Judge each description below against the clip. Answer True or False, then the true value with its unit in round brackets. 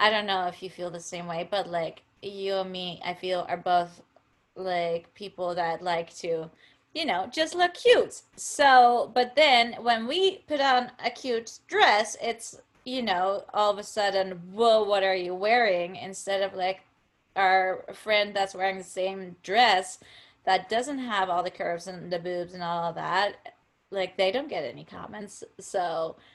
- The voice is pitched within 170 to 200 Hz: True (190 Hz)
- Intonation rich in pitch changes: False (4.5 semitones)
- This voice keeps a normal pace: True (180 wpm)